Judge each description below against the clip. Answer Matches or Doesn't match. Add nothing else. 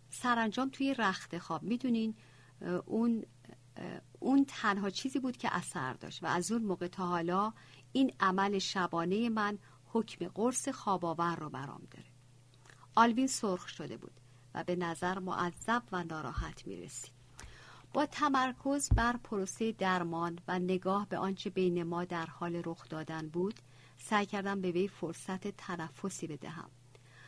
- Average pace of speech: Matches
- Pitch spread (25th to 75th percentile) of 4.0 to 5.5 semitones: Matches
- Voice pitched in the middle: Matches